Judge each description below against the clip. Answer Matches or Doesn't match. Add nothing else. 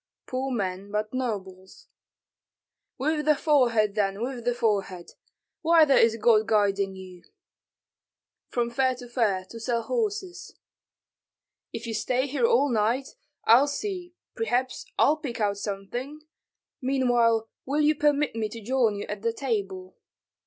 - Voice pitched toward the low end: Doesn't match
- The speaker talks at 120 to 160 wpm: Matches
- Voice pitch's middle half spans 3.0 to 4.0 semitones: Doesn't match